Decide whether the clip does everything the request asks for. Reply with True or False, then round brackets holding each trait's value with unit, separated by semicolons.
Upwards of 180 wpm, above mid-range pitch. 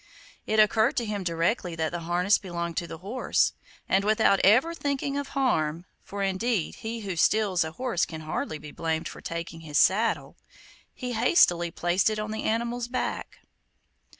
False (175 wpm; 195 Hz)